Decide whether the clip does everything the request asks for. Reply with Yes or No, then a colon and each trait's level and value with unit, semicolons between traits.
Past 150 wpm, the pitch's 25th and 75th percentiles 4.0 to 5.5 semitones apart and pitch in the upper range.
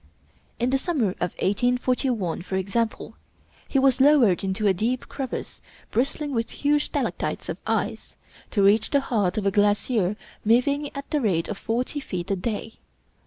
Yes: average, 165 wpm; average, 5.2 semitones; high, 230 Hz